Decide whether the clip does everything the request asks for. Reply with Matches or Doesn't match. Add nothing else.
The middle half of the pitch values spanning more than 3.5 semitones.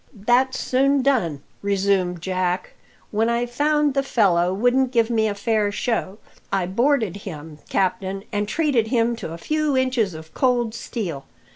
Matches